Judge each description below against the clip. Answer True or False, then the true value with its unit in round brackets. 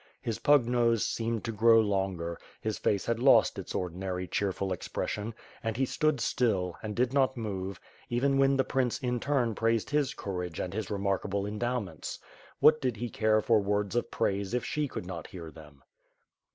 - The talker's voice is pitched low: True (110 Hz)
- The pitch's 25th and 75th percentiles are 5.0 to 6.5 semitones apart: False (4.0 semitones)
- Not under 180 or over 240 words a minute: True (185 wpm)